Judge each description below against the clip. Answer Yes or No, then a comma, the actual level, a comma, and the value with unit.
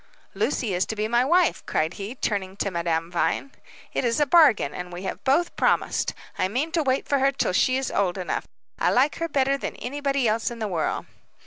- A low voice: No, high, 240 Hz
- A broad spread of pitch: Yes, wide, 6.5 semitones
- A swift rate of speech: Yes, fast, 220 wpm